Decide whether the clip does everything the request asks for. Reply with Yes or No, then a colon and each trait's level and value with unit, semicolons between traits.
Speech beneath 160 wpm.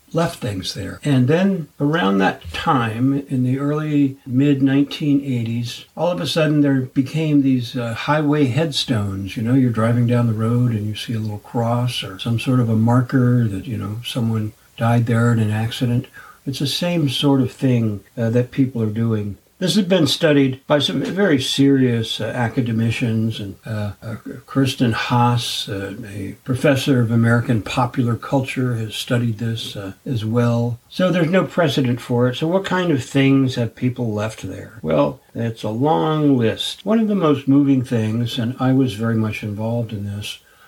No: average, 185 wpm